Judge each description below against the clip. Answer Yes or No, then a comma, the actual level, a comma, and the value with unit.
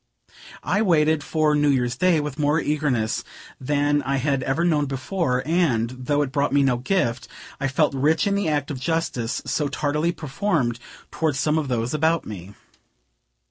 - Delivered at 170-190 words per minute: Yes, average, 175 wpm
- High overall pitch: No, medium, 145 Hz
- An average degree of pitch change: Yes, average, 3.4 semitones